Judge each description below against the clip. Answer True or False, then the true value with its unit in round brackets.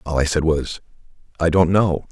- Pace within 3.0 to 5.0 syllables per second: True (4.9 syllables/s)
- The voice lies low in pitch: True (80 Hz)